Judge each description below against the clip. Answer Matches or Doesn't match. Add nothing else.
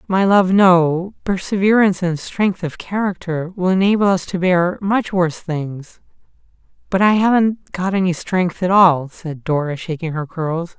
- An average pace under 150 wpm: Doesn't match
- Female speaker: Doesn't match